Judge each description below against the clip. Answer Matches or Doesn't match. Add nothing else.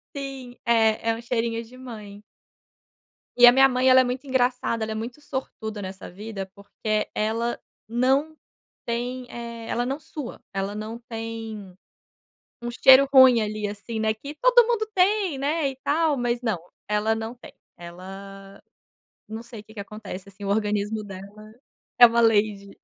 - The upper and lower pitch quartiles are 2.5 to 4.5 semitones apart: Matches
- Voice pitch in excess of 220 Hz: Matches